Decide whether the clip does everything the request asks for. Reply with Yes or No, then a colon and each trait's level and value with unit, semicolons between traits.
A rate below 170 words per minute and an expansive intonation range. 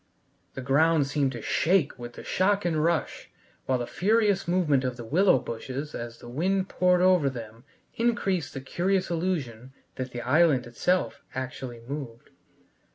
Yes: average, 160 wpm; wide, 6.2 semitones